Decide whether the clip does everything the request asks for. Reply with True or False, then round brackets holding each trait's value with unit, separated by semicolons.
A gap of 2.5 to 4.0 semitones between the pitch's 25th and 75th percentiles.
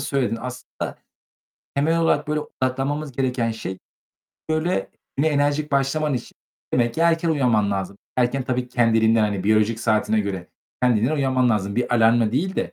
False (4.5 semitones)